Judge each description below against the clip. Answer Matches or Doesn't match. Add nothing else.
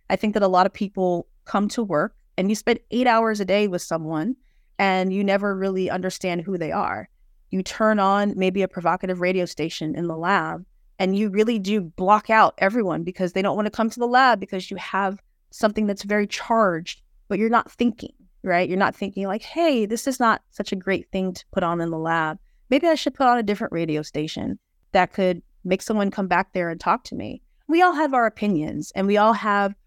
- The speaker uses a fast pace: Matches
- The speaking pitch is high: Matches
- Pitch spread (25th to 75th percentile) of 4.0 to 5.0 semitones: Doesn't match